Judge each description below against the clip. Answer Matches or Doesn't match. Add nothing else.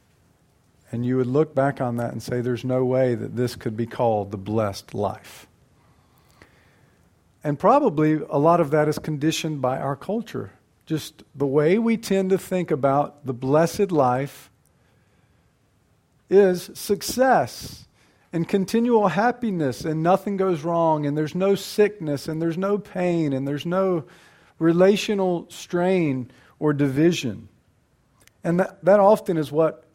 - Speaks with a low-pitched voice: Doesn't match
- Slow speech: Doesn't match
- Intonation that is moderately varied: Doesn't match